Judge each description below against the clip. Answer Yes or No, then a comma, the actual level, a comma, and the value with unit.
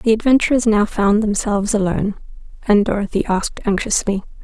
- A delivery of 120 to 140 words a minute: Yes, slow, 135 wpm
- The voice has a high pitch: Yes, high, 210 Hz